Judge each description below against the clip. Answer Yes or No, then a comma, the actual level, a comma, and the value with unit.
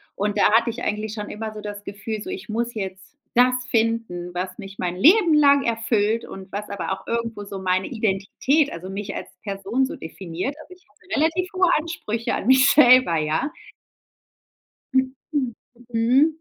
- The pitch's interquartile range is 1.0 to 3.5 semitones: No, average, 4.9 semitones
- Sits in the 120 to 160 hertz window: No, high, 225 Hz